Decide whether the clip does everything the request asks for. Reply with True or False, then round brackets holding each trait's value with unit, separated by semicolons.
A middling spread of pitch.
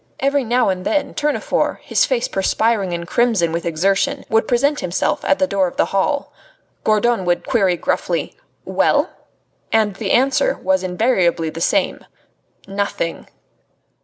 False (6.1 semitones)